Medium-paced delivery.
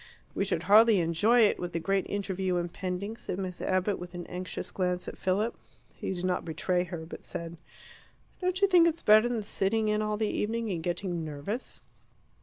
Yes: average, 195 wpm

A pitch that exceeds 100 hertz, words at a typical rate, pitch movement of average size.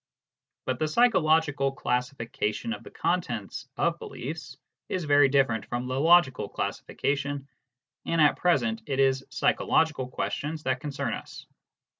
No: medium, 140 Hz; slow, 130 wpm; average, 3.4 semitones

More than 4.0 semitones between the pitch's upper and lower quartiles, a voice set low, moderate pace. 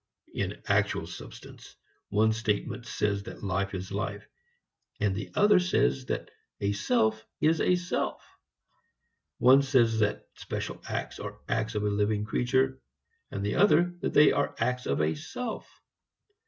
Yes: average, 4.6 semitones; low, 110 Hz; average, 150 wpm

